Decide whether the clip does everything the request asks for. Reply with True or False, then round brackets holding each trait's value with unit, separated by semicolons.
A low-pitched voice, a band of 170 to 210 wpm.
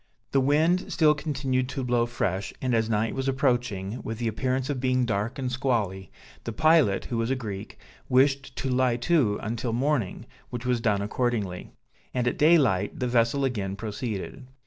True (125 Hz; 175 wpm)